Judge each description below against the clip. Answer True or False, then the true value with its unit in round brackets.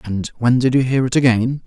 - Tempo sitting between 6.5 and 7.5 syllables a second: False (5.4 syllables/s)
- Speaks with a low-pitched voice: True (125 Hz)